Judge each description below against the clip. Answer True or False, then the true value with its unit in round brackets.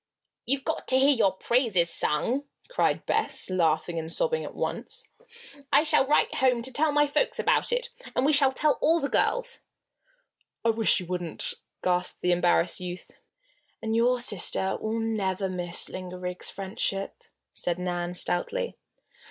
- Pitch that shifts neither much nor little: False (7.5 semitones)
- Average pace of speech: True (155 wpm)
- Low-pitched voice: False (220 Hz)